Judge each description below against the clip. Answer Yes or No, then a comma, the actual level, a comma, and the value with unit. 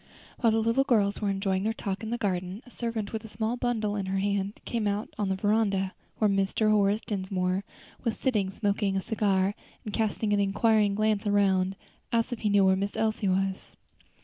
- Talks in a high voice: Yes, high, 205 Hz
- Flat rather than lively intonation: Yes, narrow, 2.2 semitones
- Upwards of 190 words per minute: Yes, average, 200 wpm